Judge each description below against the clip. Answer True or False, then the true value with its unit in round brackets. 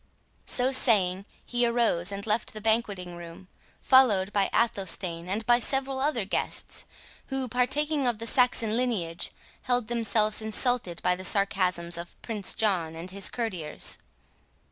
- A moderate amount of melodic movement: True (4.8 semitones)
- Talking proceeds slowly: False (145 wpm)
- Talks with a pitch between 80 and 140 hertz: False (215 Hz)